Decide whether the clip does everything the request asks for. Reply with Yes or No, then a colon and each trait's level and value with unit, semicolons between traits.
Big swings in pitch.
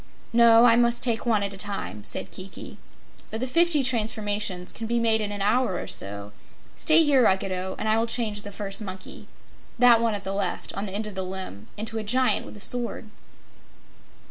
No: average, 3.2 semitones